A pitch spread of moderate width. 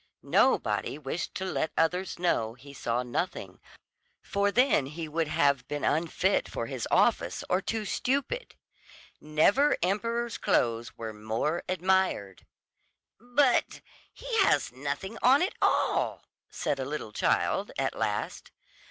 No: wide, 8.4 semitones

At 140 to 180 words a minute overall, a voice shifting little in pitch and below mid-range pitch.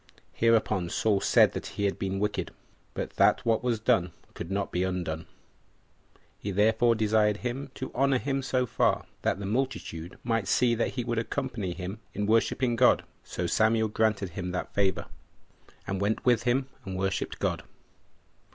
No: average, 170 wpm; average, 3.7 semitones; low, 110 Hz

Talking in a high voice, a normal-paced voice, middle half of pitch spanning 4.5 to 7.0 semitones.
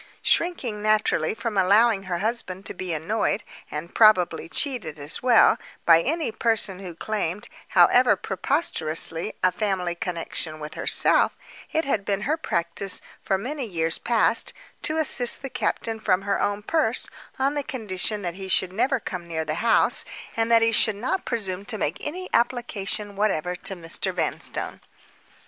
Yes: high, 205 Hz; average, 160 wpm; average, 4.8 semitones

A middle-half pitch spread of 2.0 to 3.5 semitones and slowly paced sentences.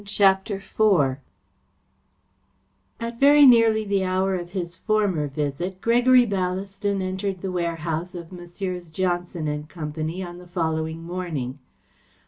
Yes: average, 3.1 semitones; slow, 120 wpm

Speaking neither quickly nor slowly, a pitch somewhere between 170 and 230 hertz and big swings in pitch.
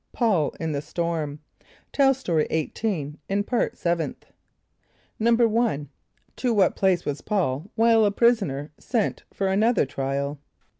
No: slow, 130 wpm; high, 190 Hz; wide, 7.1 semitones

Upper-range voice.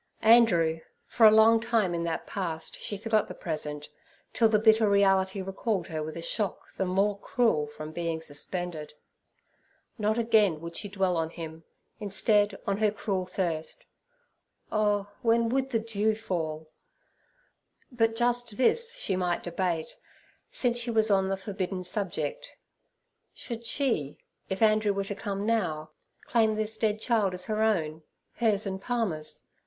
Yes: high, 200 Hz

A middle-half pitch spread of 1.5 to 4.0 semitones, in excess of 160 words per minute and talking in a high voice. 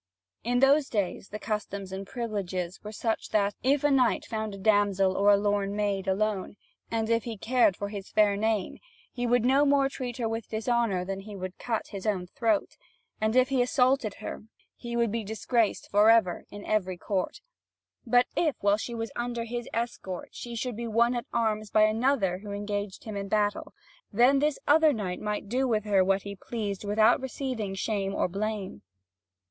Yes: average, 3.0 semitones; average, 190 wpm; high, 215 Hz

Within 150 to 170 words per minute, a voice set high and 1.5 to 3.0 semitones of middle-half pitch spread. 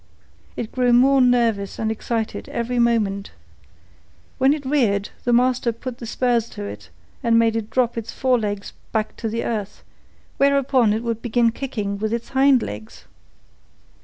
Yes: average, 160 wpm; high, 235 Hz; narrow, 2.5 semitones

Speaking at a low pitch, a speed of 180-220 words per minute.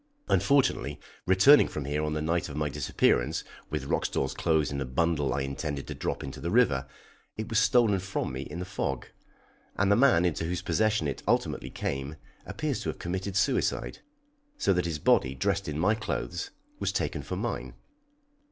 Yes: very low, 85 Hz; average, 185 wpm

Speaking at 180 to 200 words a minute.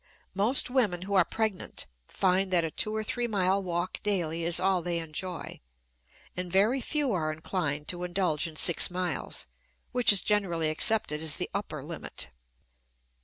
No: average, 165 wpm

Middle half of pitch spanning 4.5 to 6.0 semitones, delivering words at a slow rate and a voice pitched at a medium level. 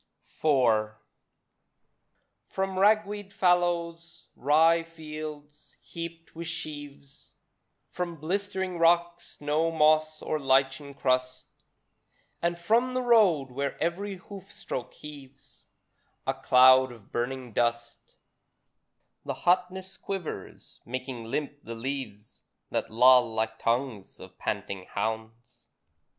Yes: average, 5.2 semitones; slow, 105 wpm; medium, 150 Hz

